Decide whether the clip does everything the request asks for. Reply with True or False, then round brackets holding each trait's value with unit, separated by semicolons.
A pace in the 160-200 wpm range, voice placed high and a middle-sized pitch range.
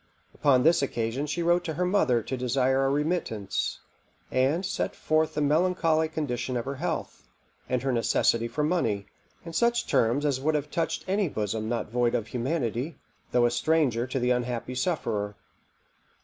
False (170 wpm; 135 Hz; 5.0 semitones)